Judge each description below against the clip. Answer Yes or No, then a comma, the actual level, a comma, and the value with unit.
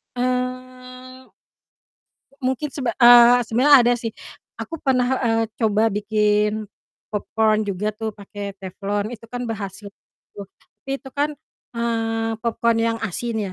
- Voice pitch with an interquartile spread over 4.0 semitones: No, average, 3.1 semitones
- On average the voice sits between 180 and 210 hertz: No, high, 225 Hz